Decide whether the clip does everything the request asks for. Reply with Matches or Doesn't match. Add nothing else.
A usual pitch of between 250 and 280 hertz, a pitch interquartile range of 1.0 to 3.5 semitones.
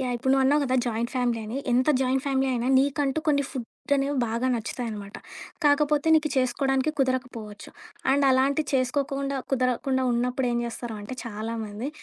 Matches